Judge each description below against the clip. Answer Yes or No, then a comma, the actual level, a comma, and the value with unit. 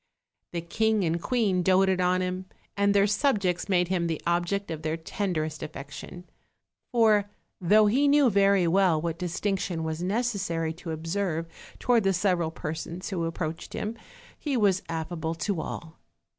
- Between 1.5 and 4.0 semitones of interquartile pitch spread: Yes, average, 3.5 semitones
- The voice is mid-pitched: Yes, medium, 180 Hz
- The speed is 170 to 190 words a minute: No, average, 160 wpm